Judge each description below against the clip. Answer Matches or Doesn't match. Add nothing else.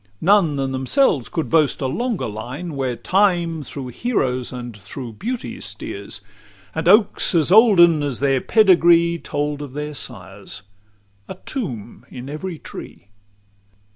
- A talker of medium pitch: Matches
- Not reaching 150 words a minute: Matches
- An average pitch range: Doesn't match